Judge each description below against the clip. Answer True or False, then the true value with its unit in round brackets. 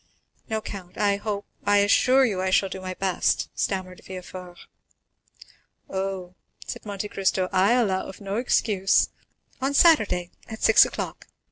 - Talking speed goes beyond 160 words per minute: False (135 wpm)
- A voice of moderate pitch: False (195 Hz)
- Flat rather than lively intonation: True (2.3 semitones)